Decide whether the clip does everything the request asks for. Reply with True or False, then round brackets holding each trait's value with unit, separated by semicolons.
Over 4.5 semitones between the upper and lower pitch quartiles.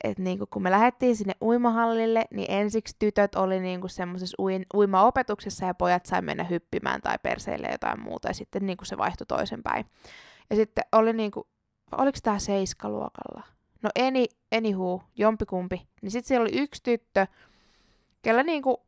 False (3.7 semitones)